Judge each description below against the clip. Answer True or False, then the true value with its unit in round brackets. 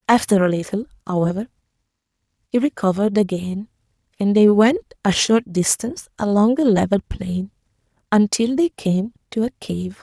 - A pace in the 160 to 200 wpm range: False (140 wpm)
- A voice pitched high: True (215 Hz)